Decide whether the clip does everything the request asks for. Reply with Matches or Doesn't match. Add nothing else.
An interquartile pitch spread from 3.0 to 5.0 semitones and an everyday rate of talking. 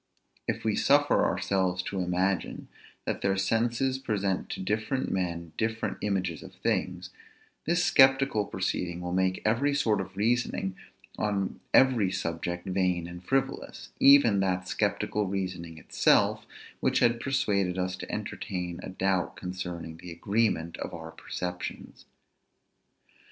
Doesn't match